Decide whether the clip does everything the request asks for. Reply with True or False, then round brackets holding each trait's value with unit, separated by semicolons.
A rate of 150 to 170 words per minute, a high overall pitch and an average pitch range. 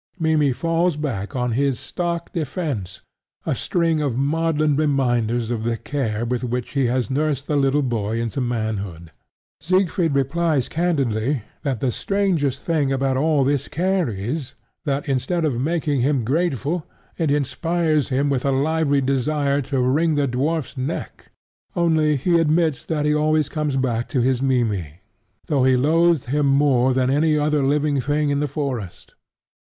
False (160 wpm; 140 Hz; 3.6 semitones)